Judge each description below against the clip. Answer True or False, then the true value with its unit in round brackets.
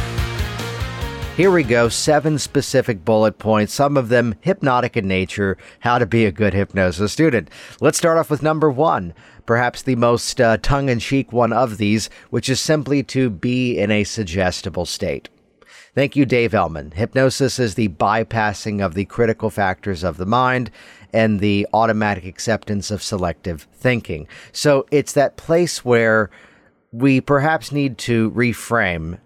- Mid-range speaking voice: False (115 Hz)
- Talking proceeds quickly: False (160 wpm)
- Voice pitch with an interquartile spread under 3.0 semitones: False (4.1 semitones)